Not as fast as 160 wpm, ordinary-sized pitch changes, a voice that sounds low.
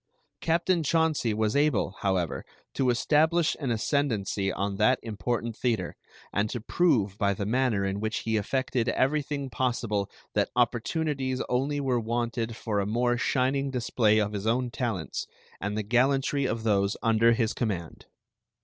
Yes: average, 150 wpm; average, 3.9 semitones; low, 120 Hz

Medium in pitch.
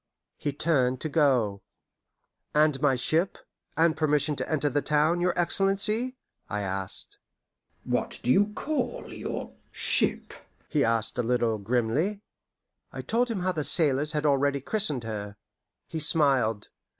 Yes: medium, 145 Hz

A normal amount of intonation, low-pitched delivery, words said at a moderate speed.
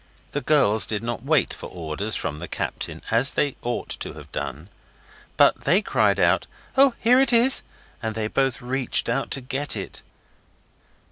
Yes: average, 5.0 semitones; low, 125 Hz; average, 175 wpm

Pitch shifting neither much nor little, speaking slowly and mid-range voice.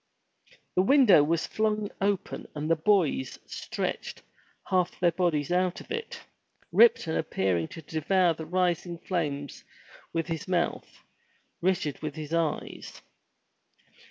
Yes: average, 3.1 semitones; slow, 125 wpm; medium, 170 Hz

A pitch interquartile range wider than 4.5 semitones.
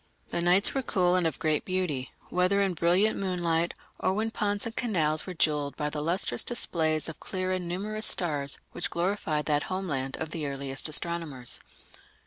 No: average, 3.7 semitones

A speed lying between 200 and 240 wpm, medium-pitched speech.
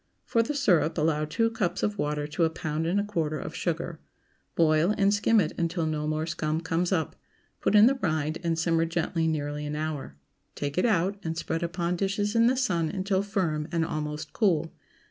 Yes: fast, 205 wpm; medium, 165 Hz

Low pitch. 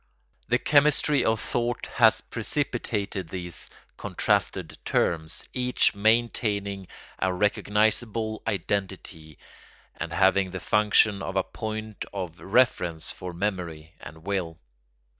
Yes: low, 100 Hz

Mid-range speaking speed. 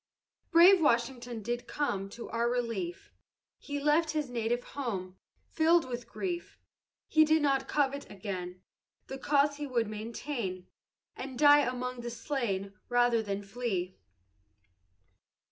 No: slow, 130 wpm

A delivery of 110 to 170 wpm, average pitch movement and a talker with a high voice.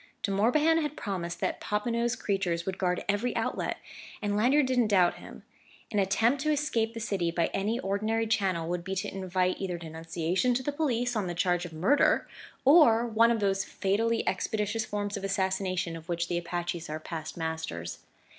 No: average, 185 wpm; average, 4.7 semitones; high, 195 Hz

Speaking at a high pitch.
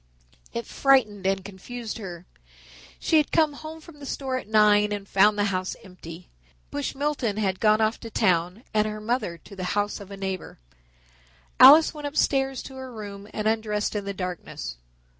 Yes: high, 210 Hz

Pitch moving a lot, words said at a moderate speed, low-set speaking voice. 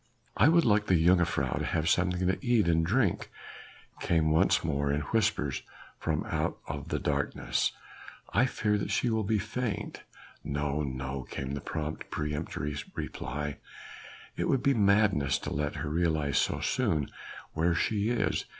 Yes: wide, 6.0 semitones; average, 155 wpm; very low, 85 Hz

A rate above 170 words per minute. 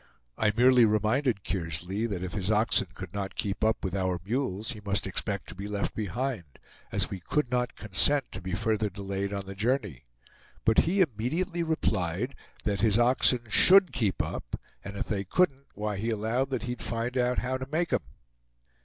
Yes: average, 190 wpm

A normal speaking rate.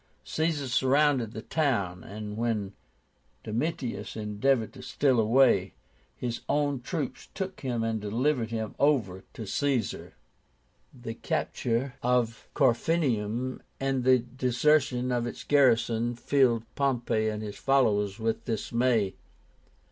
No: slow, 115 wpm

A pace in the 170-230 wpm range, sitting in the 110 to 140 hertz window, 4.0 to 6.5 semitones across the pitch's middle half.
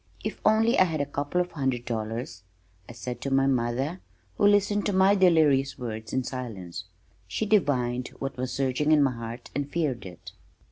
Yes: average, 185 wpm; low, 135 Hz; wide, 5.5 semitones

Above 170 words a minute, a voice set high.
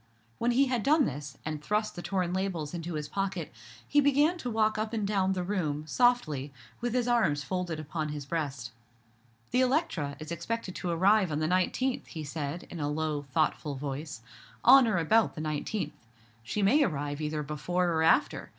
No: average, 185 wpm; medium, 175 Hz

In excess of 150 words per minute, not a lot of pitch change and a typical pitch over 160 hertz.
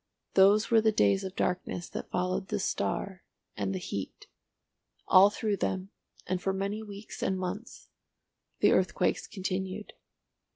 No: average, 140 wpm; narrow, 1.9 semitones; high, 190 Hz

